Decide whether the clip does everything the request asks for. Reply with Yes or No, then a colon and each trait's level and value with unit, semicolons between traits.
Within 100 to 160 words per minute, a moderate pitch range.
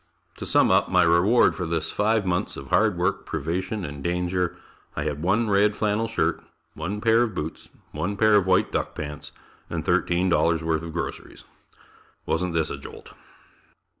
No: average, 170 wpm; average, 4.0 semitones